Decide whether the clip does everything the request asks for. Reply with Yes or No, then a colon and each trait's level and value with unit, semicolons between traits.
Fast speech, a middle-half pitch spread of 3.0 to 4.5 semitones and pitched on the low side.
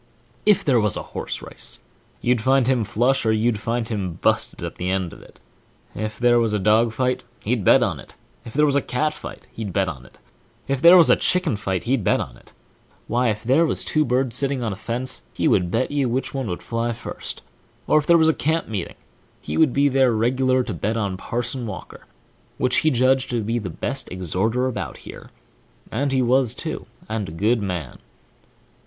Yes: fast, 220 wpm; average, 3.9 semitones; low, 120 Hz